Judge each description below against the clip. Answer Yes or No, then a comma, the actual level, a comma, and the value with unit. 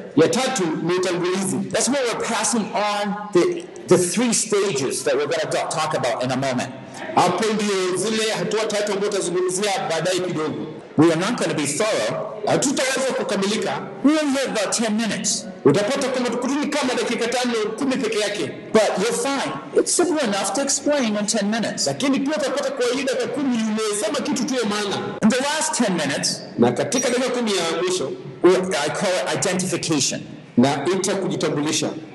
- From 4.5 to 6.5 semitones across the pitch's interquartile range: Yes, wide, 5.6 semitones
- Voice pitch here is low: No, high, 215 Hz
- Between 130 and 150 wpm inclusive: No, average, 120 wpm